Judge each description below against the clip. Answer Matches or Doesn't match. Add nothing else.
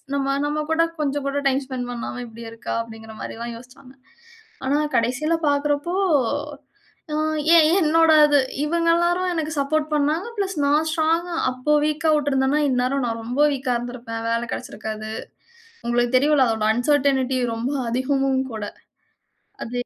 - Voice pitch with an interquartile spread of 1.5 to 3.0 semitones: Doesn't match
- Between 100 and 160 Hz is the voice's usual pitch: Doesn't match